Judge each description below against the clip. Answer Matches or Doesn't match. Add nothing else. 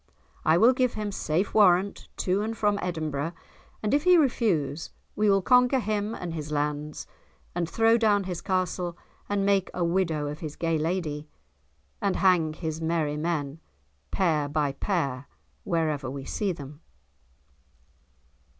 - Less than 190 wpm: Matches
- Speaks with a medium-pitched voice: Matches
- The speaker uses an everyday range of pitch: Matches